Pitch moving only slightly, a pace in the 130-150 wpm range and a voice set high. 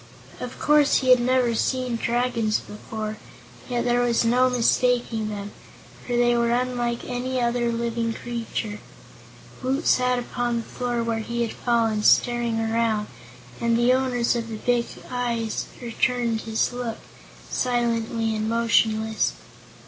Yes: narrow, 1.5 semitones; average, 140 wpm; high, 235 Hz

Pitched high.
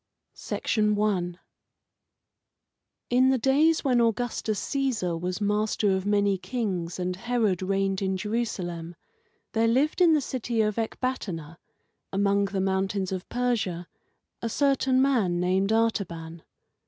Yes: high, 205 Hz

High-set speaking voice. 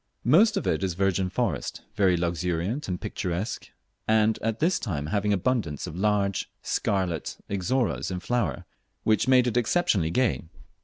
No: low, 100 Hz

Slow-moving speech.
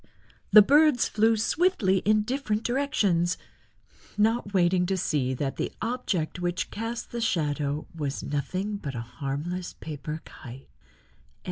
Yes: slow, 130 wpm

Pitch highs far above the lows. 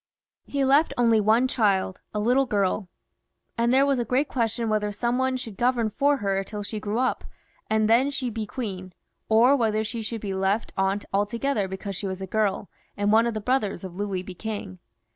No: average, 3.4 semitones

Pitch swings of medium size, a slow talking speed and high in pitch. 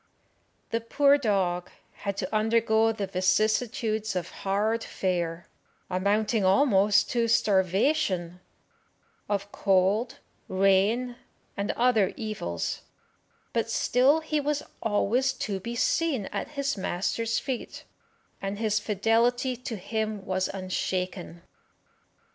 Yes: average, 3.6 semitones; slow, 105 wpm; high, 215 Hz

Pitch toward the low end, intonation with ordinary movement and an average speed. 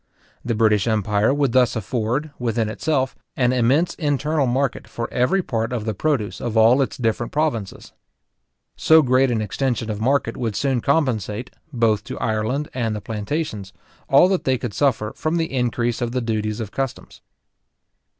Yes: low, 120 Hz; average, 3.8 semitones; average, 170 wpm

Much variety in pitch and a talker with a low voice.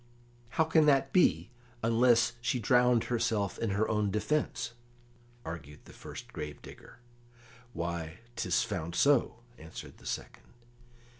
Yes: wide, 6.4 semitones; low, 115 Hz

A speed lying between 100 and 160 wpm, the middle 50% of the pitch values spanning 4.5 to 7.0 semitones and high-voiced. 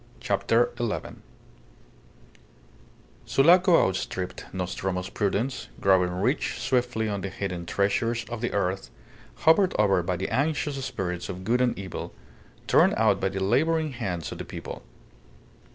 No: slow, 135 wpm; average, 5.2 semitones; low, 100 Hz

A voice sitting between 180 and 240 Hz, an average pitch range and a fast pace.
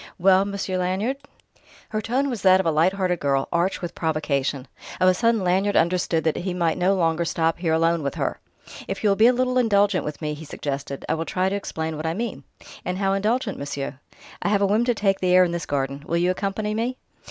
Yes: medium, 185 Hz; average, 3.8 semitones; fast, 235 wpm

